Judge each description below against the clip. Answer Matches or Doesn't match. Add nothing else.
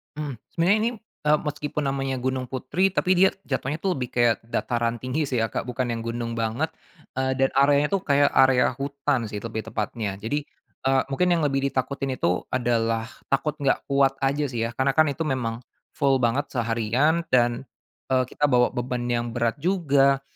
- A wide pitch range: Doesn't match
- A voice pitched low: Matches